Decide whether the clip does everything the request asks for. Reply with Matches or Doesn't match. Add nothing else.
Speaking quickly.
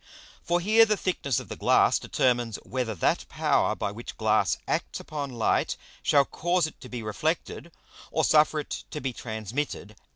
Doesn't match